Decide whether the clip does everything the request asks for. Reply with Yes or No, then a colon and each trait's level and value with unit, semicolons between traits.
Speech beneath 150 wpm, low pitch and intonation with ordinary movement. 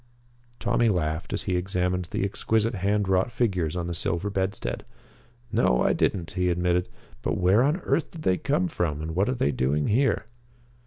No: average, 180 wpm; very low, 90 Hz; average, 4.0 semitones